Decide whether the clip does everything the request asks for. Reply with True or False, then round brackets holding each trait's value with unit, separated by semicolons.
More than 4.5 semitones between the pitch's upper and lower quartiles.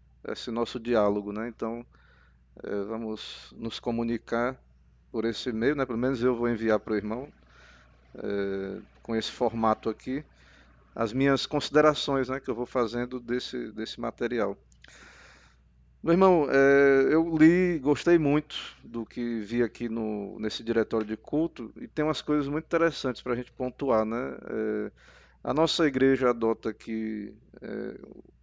False (3.9 semitones)